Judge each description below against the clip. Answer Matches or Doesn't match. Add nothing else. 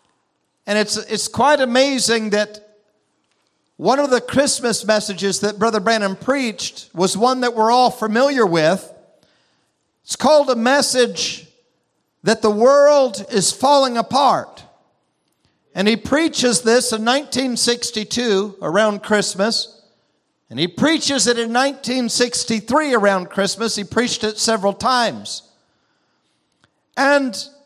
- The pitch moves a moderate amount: Matches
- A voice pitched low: Doesn't match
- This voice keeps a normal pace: Doesn't match